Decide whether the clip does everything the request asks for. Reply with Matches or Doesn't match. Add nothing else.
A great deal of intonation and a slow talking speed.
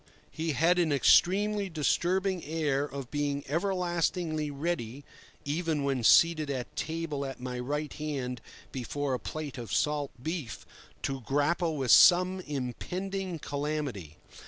Doesn't match